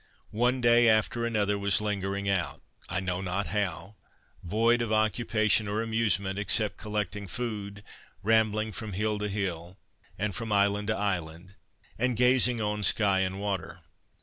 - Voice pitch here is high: No, low, 105 Hz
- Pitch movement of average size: No, narrow, 2.2 semitones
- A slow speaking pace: No, average, 150 wpm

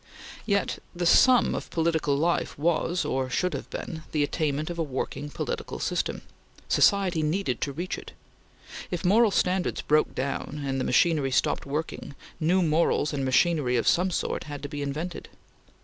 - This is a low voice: No, medium, 160 Hz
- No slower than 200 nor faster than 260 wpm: No, average, 165 wpm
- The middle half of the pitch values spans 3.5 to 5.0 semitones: Yes, average, 3.8 semitones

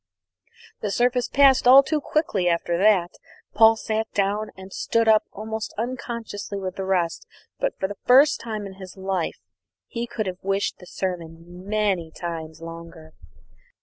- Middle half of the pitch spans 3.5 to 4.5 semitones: Yes, average, 3.9 semitones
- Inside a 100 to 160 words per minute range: Yes, average, 155 wpm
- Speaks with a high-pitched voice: Yes, high, 200 Hz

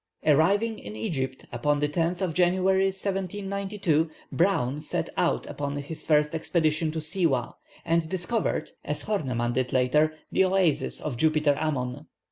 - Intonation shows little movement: No, average, 4.6 semitones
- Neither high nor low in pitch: Yes, medium, 160 Hz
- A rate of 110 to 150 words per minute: Yes, average, 140 wpm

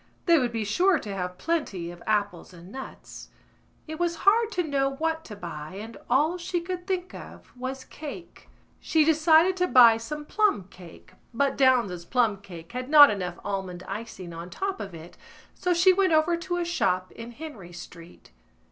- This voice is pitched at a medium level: No, very high, 255 Hz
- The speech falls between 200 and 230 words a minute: No, average, 175 wpm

